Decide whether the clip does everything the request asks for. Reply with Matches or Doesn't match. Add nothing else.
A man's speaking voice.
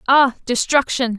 Doesn't match